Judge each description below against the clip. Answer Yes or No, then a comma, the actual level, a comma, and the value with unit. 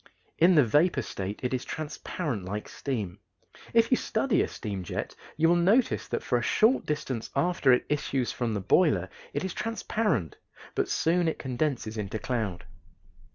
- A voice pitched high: No, low, 135 Hz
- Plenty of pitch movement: Yes, wide, 8.1 semitones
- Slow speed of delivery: No, average, 170 wpm